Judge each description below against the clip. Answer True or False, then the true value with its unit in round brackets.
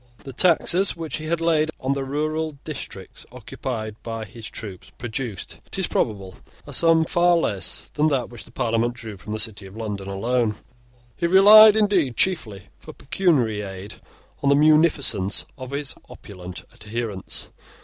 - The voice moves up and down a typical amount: False (6.8 semitones)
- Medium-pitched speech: False (125 Hz)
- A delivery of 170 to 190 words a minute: False (160 wpm)